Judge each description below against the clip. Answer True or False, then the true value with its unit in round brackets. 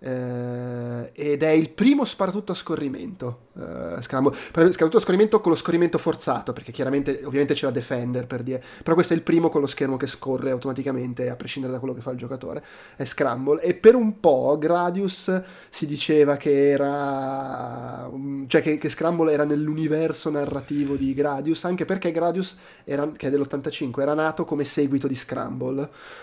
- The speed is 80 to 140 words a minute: False (170 wpm)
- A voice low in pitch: False (145 Hz)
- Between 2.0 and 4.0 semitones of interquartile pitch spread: True (3.5 semitones)